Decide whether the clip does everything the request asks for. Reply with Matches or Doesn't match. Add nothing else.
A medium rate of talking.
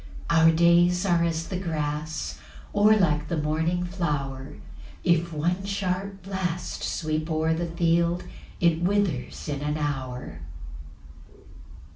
Doesn't match